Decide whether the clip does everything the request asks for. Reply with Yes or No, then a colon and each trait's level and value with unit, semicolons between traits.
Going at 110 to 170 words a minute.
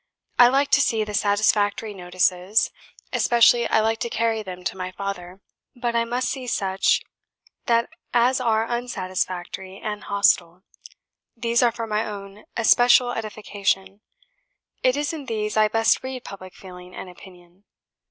Yes: average, 145 wpm